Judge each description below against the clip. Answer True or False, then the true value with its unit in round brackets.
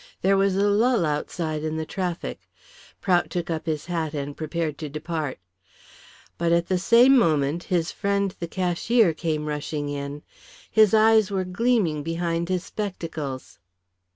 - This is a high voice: False (170 Hz)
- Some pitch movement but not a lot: True (4.0 semitones)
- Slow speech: False (150 wpm)